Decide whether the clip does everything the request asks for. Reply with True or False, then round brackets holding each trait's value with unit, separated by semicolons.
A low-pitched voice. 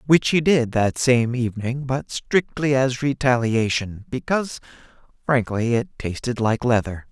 True (125 Hz)